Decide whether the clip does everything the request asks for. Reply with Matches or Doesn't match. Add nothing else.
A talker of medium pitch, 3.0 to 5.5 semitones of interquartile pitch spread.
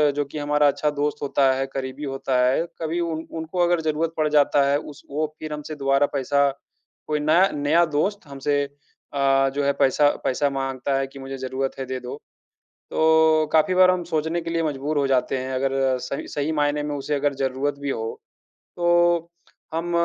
Doesn't match